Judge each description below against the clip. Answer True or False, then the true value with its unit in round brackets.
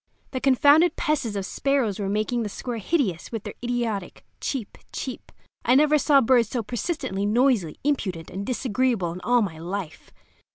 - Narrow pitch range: False (5.1 semitones)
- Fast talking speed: False (165 wpm)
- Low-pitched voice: False (235 Hz)